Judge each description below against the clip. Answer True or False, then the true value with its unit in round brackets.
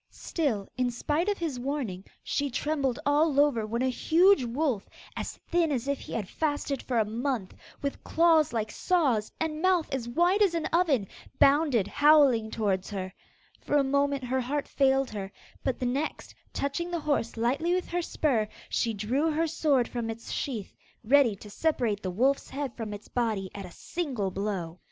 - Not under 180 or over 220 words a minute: True (185 wpm)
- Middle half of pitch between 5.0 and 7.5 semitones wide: True (5.3 semitones)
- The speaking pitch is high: True (265 Hz)